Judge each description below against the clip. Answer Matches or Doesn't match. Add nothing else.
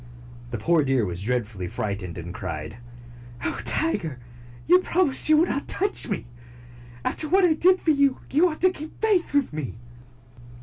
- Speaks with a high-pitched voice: Matches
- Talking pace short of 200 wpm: Matches